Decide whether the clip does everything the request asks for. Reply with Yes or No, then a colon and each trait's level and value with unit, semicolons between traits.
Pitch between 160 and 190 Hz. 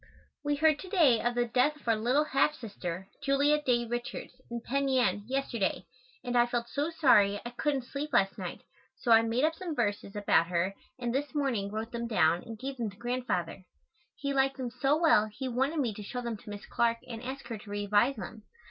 No: high, 240 Hz